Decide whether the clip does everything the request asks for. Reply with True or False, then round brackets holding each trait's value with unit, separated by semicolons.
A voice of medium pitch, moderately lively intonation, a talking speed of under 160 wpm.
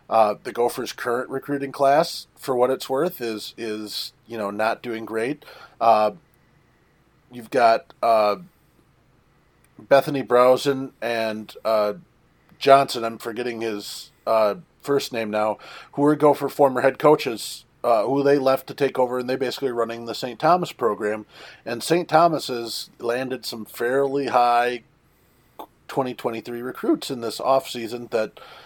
False (125 Hz; 3.3 semitones; 145 wpm)